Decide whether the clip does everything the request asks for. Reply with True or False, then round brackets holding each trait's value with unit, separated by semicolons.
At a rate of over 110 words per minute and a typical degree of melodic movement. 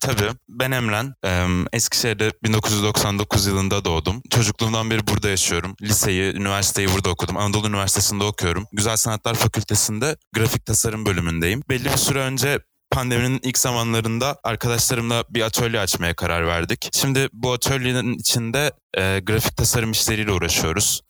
True (135 wpm; 3.3 semitones)